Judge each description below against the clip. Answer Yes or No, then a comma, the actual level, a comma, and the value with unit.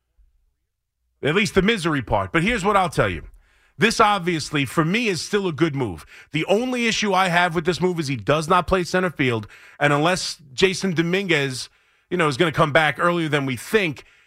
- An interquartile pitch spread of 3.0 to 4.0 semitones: No, wide, 5.6 semitones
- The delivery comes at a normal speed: No, fast, 210 wpm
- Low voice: No, medium, 170 Hz